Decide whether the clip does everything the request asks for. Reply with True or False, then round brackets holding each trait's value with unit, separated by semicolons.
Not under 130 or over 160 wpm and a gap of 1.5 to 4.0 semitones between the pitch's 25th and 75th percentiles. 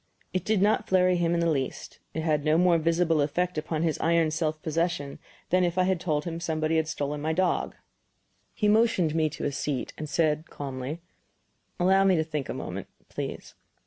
False (200 wpm; 2.7 semitones)